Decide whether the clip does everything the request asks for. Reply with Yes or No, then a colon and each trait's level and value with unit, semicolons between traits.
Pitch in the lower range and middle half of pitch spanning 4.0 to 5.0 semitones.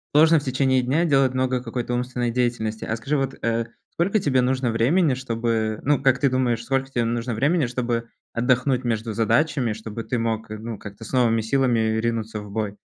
No: low, 120 Hz; average, 2.7 semitones